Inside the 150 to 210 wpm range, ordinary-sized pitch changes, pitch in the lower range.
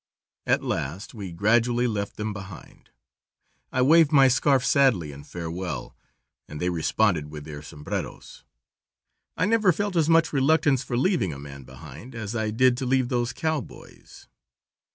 No: average, 155 wpm; wide, 7.8 semitones; low, 115 Hz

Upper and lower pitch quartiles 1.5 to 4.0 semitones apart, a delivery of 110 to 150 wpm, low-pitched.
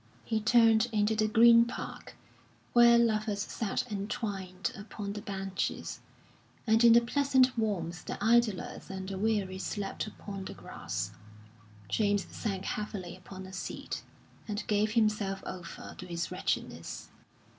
No: average, 2.7 semitones; slow, 135 wpm; high, 210 Hz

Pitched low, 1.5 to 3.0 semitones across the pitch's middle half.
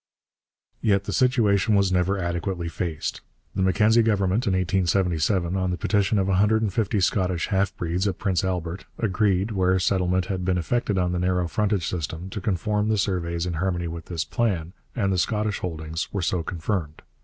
Yes: very low, 95 Hz; narrow, 2.5 semitones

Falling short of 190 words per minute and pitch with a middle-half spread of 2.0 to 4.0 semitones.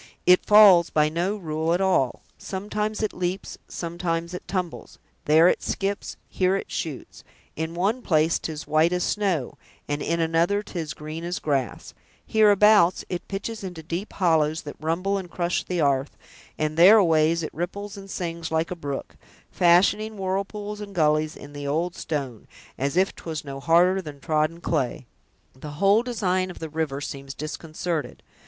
Yes: average, 165 wpm; average, 3.7 semitones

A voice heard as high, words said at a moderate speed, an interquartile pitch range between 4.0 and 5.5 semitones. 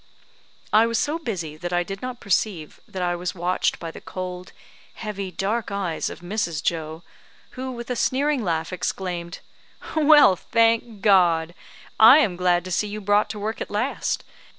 Yes: high, 195 Hz; average, 175 wpm; average, 4.5 semitones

